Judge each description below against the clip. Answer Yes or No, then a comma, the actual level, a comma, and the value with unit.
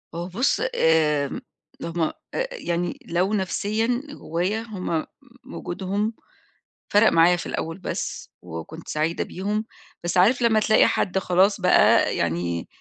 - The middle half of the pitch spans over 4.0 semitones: Yes, average, 4.4 semitones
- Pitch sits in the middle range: Yes, medium, 180 Hz